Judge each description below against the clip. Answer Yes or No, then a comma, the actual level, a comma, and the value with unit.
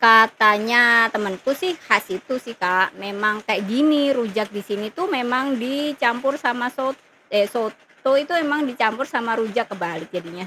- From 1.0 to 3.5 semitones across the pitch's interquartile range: No, average, 4.2 semitones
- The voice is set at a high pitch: Yes, high, 235 Hz